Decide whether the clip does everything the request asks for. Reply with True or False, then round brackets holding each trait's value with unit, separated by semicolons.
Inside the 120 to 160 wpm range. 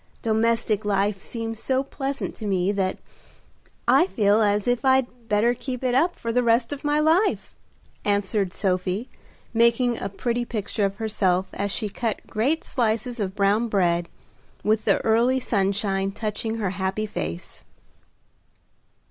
True (150 wpm)